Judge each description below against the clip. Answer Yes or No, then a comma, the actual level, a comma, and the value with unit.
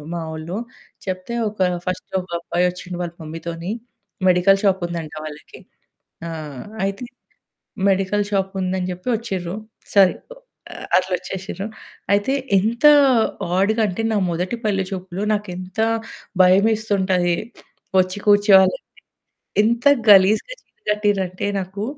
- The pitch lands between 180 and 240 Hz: Yes, high, 190 Hz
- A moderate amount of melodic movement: No, narrow, 2.1 semitones